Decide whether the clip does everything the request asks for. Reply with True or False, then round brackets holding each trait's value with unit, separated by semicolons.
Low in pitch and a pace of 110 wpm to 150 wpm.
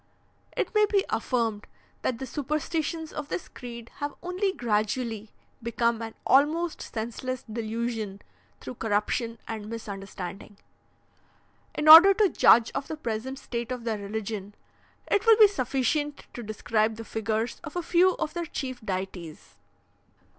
False (235 Hz; 140 wpm)